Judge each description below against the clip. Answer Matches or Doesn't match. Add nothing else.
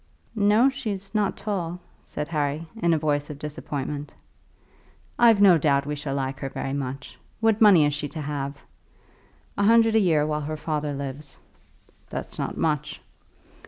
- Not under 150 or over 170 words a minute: Matches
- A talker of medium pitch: Matches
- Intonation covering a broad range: Matches